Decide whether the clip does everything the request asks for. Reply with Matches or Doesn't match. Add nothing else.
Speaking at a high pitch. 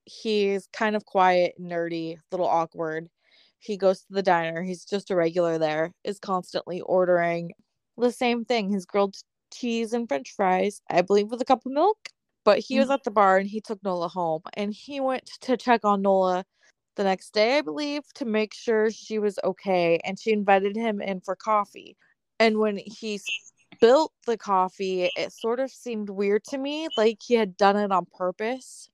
Matches